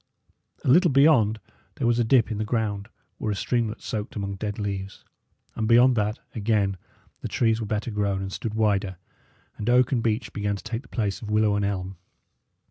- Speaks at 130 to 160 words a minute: No, average, 200 wpm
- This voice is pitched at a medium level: No, low, 110 Hz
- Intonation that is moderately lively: No, narrow, 2.3 semitones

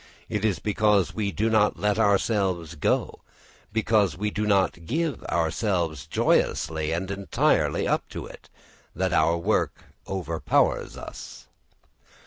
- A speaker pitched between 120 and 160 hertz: No, low, 100 Hz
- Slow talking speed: Yes, slow, 125 wpm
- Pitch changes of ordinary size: Yes, average, 3.9 semitones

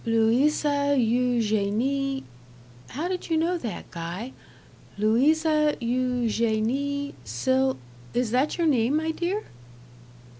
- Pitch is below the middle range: No, very high, 260 Hz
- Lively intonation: No, average, 4.7 semitones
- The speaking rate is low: Yes, slow, 100 wpm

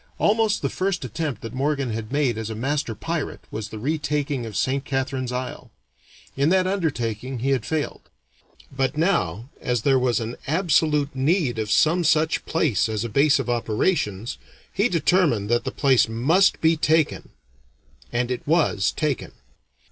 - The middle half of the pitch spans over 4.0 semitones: Yes, average, 5.1 semitones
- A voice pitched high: No, low, 135 Hz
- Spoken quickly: No, average, 165 wpm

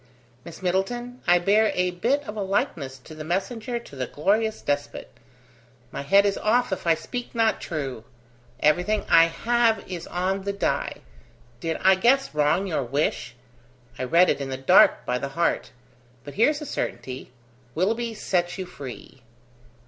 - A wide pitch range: Yes, wide, 6.4 semitones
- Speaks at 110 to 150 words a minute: No, average, 165 wpm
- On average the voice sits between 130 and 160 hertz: No, medium, 180 Hz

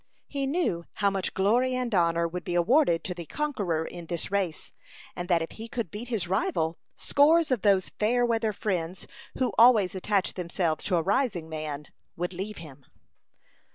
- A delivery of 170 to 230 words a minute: Yes, average, 180 wpm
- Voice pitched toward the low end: No, high, 190 Hz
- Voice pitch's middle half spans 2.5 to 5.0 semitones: No, wide, 5.4 semitones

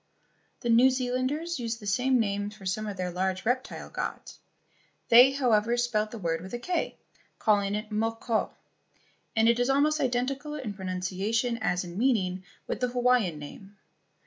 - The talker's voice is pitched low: No, high, 225 Hz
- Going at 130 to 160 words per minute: No, average, 170 wpm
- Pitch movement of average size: Yes, average, 4.0 semitones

